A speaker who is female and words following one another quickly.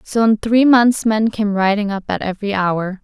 Yes: female; fast, 220 wpm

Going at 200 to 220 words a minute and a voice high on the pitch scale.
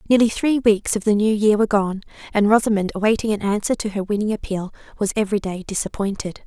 Yes: fast, 205 wpm; high, 210 Hz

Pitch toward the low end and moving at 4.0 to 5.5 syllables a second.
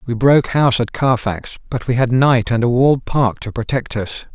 Yes: low, 120 Hz; 5.4 syllables/s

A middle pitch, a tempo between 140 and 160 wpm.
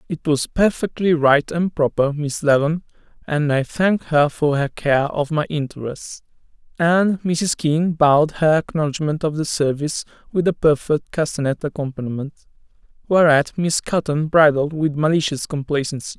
Yes: medium, 155 Hz; average, 145 wpm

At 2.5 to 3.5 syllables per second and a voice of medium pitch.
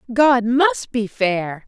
No: 2.9 syllables/s; high, 225 Hz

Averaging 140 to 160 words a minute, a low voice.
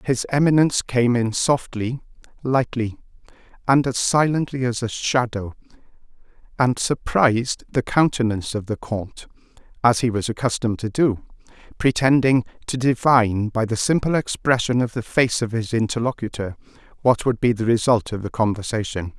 Yes: average, 145 wpm; low, 120 Hz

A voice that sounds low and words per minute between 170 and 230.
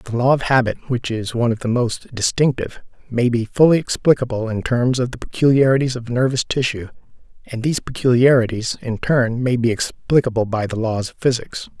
Yes: low, 120 Hz; average, 185 wpm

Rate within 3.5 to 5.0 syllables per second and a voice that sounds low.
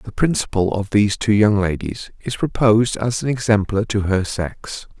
Yes: 4.8 syllables/s; low, 105 Hz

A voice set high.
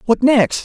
Yes: high, 240 Hz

